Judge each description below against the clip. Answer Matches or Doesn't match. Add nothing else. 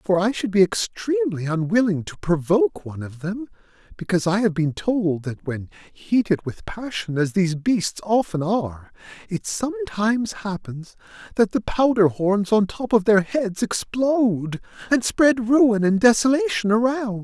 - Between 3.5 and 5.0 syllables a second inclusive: Matches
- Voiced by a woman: Doesn't match